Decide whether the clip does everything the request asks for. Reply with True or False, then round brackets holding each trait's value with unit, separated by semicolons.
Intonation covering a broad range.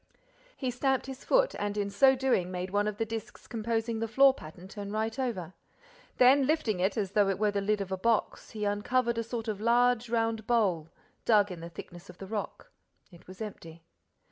False (3.3 semitones)